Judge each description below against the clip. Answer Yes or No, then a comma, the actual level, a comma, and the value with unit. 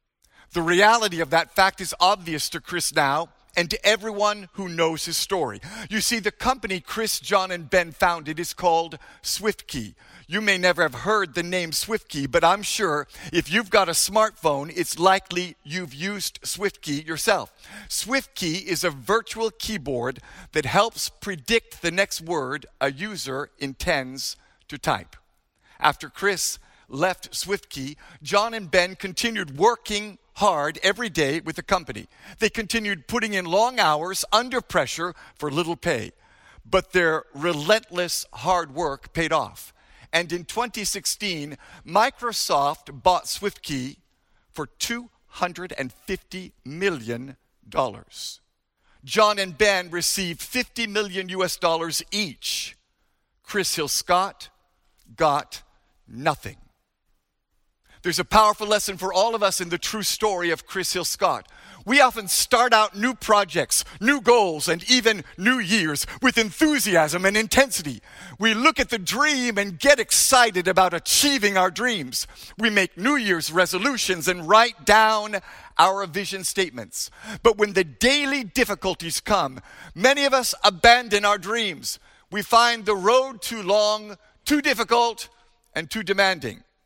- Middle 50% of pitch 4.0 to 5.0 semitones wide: Yes, average, 4.6 semitones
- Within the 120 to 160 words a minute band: Yes, average, 140 wpm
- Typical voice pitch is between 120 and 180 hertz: No, high, 190 Hz